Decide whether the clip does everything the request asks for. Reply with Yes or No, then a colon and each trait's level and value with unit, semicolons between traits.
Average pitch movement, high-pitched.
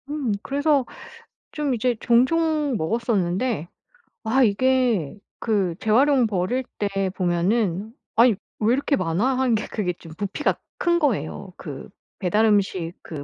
No: wide, 5.7 semitones; high, 220 Hz